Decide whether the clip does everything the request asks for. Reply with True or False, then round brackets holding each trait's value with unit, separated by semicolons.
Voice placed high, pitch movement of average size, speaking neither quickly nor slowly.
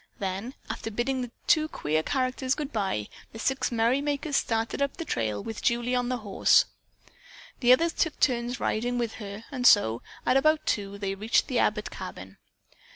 True (240 Hz; 4.6 semitones; 180 wpm)